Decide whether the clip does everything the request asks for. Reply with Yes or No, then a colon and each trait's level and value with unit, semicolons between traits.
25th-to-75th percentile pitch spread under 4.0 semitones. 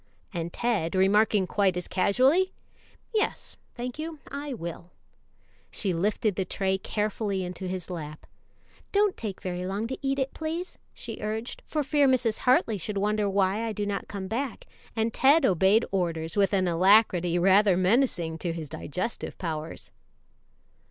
No: average, 4.7 semitones